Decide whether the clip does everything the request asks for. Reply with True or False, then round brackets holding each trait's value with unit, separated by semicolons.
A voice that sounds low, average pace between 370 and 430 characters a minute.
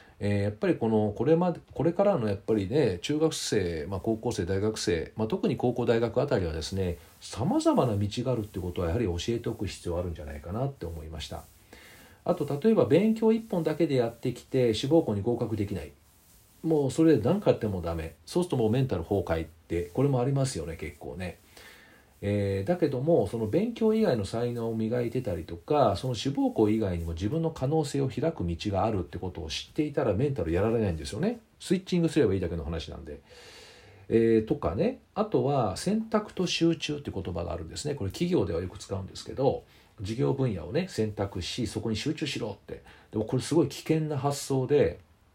True (115 Hz; 410 characters per minute)